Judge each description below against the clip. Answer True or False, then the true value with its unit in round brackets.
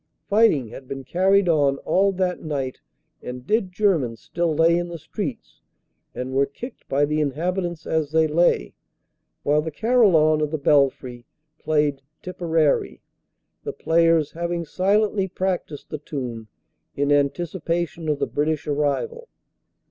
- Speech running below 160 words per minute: True (140 wpm)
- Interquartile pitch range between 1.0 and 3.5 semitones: False (3.9 semitones)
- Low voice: False (160 Hz)